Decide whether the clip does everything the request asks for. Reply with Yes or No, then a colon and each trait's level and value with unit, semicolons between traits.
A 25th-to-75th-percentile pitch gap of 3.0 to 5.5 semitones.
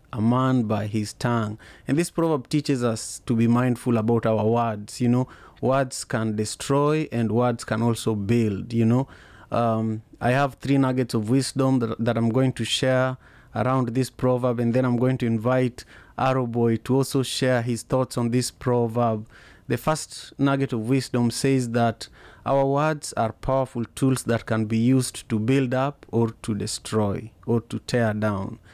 No: narrow, 2.5 semitones